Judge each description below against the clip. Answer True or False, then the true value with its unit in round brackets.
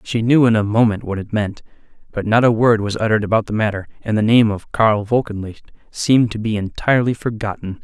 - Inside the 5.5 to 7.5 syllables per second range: True (5.9 syllables/s)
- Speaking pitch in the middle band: False (110 Hz)